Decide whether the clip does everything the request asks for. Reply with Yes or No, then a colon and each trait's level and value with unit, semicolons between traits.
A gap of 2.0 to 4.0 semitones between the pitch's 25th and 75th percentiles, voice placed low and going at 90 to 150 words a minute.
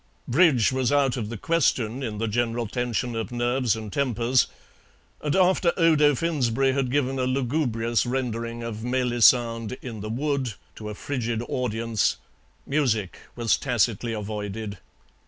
Yes: average, 2.8 semitones; low, 120 Hz; average, 140 wpm